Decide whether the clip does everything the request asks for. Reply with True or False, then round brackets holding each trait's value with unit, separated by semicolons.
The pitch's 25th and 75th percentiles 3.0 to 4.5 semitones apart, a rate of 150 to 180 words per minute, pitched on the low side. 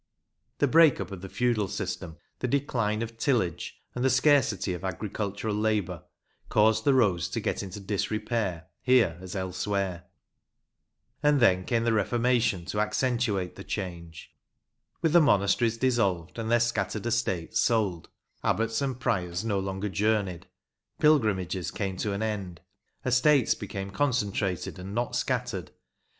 False (4.1 semitones; 140 wpm; 105 Hz)